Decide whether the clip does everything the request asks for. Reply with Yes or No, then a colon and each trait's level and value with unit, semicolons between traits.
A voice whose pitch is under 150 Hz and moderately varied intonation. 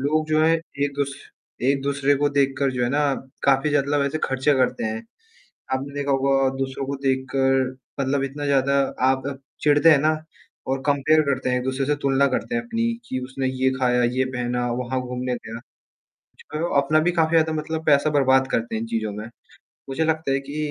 No: low, 135 Hz; narrow, 1.9 semitones